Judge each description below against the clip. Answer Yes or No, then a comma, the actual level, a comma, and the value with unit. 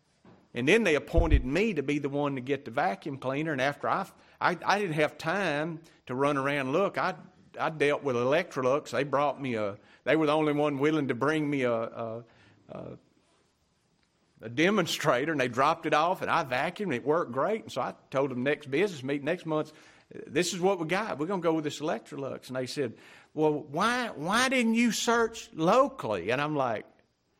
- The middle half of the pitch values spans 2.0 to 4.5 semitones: Yes, average, 4.1 semitones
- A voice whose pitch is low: No, medium, 150 Hz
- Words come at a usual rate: No, fast, 210 wpm